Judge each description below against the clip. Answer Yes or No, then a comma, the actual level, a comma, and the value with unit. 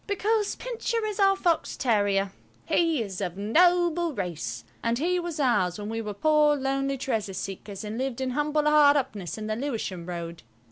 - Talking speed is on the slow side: No, average, 180 wpm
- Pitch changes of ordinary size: No, wide, 8.0 semitones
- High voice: Yes, very high, 265 Hz